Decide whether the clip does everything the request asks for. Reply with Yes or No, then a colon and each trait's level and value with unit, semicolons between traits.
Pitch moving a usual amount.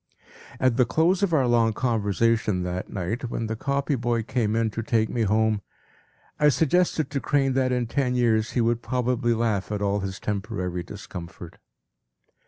Yes: average, 3.4 semitones